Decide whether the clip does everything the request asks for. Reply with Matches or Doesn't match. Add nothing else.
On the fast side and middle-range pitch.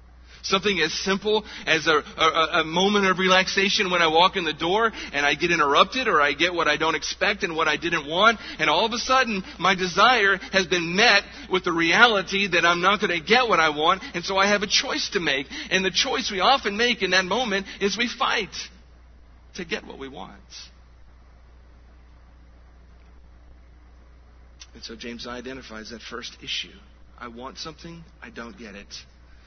Doesn't match